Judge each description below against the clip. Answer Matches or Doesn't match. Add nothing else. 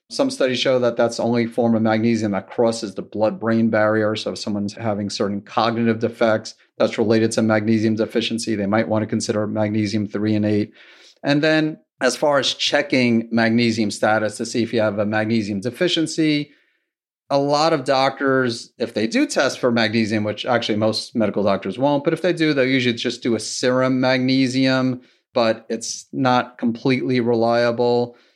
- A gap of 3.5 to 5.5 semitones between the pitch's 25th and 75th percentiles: Doesn't match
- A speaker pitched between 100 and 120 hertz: Matches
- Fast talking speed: Doesn't match